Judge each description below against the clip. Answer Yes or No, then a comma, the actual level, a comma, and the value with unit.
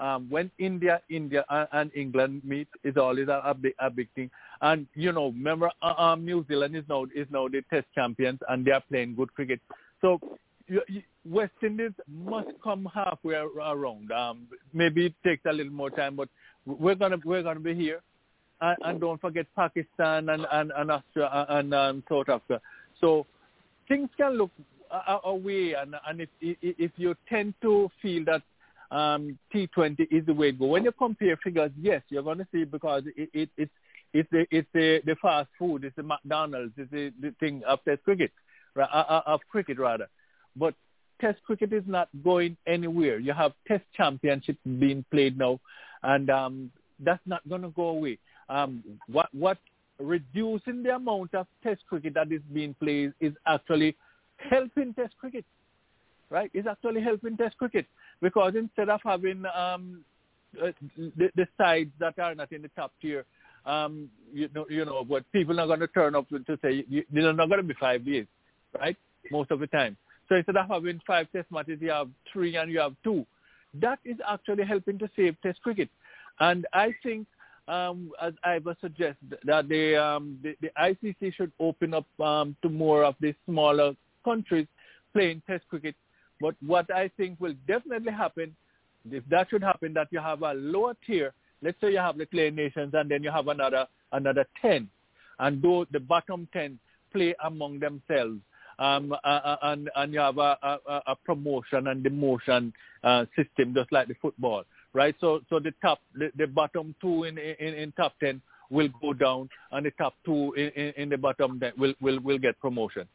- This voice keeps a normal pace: Yes, average, 185 wpm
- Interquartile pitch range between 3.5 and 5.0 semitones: Yes, average, 3.9 semitones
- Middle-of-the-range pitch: Yes, medium, 155 Hz